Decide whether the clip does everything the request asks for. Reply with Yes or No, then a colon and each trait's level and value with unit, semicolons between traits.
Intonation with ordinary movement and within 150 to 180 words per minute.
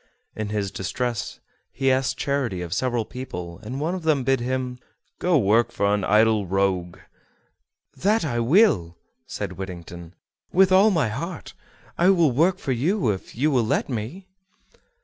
No: wide, 7.4 semitones; average, 165 wpm